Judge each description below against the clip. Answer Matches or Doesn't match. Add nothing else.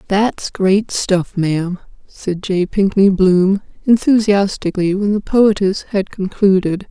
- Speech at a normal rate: Doesn't match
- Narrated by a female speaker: Matches